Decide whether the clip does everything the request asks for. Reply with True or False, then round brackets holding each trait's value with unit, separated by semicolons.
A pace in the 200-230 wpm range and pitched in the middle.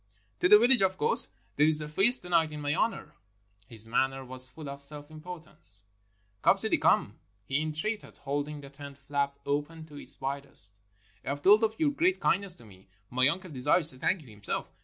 True (205 wpm; 150 Hz)